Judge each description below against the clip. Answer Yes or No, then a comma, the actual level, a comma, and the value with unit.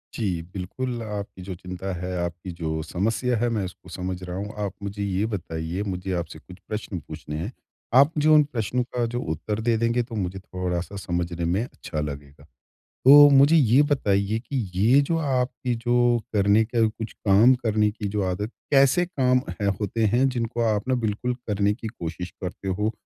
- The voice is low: Yes, low, 105 Hz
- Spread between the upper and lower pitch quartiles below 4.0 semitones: No, average, 4.9 semitones